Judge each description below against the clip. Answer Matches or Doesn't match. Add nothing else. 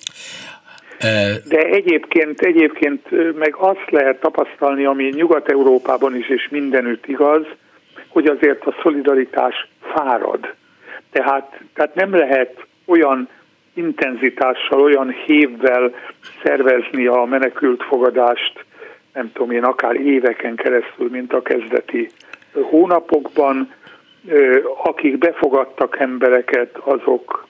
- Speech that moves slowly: Matches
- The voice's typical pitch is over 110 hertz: Matches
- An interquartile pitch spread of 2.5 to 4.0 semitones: Doesn't match